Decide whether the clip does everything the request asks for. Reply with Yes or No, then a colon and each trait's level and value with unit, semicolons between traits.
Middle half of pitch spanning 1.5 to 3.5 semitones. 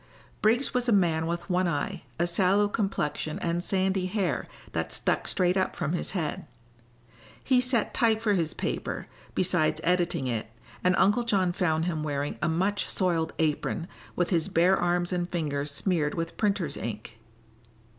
Yes: average, 3.2 semitones